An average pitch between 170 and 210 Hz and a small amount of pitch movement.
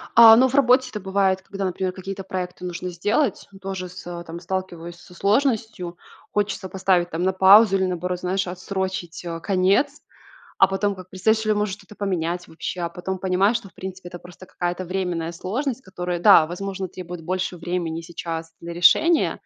Yes: medium, 185 Hz; narrow, 2.1 semitones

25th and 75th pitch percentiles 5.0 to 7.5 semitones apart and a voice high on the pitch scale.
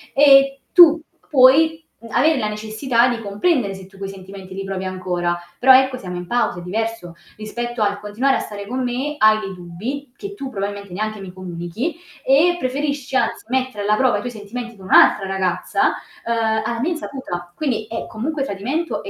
Yes: wide, 5.4 semitones; high, 225 Hz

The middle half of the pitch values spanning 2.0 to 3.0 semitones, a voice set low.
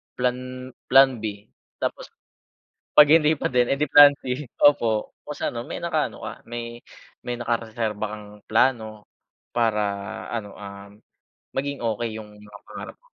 No: average, 3.5 semitones; low, 120 Hz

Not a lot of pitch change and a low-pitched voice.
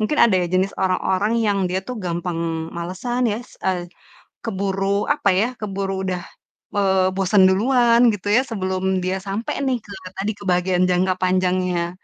No: narrow, 2.2 semitones; high, 190 Hz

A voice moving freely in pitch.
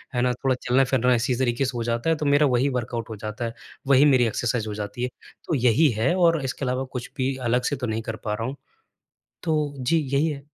No: average, 3.0 semitones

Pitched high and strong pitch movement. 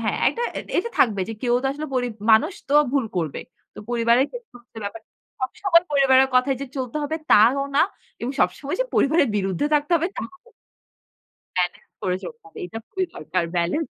Yes: very high, 265 Hz; wide, 5.8 semitones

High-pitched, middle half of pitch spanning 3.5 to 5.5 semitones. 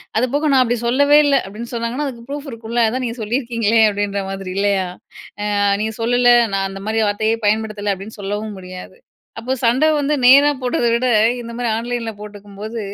No: high, 230 Hz; average, 3.1 semitones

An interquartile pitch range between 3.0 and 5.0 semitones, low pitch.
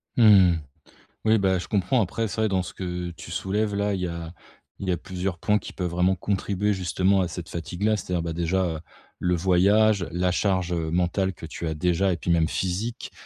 No: narrow, 2.4 semitones; very low, 90 Hz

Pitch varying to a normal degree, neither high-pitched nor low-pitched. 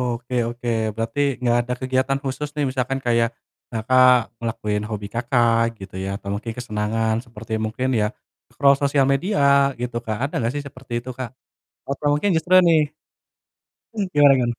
No: average, 3.2 semitones; low, 125 Hz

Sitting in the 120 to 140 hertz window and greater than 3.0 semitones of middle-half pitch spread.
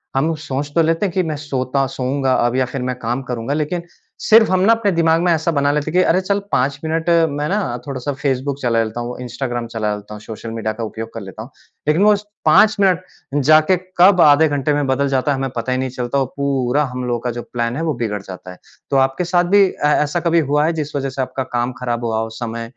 Yes: low, 135 Hz; average, 4.7 semitones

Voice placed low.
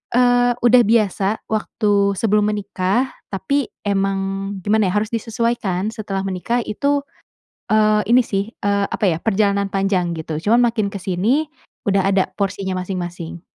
No: high, 200 Hz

